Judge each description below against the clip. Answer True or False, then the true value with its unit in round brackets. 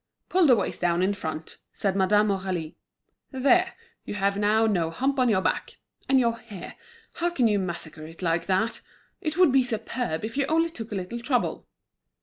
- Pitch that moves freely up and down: True (5.7 semitones)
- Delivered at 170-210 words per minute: True (190 wpm)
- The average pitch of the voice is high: True (215 Hz)